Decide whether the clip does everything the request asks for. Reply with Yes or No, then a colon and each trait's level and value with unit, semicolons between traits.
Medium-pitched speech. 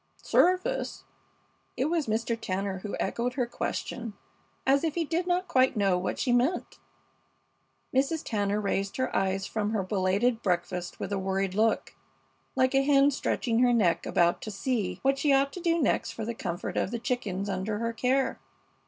No: high, 230 Hz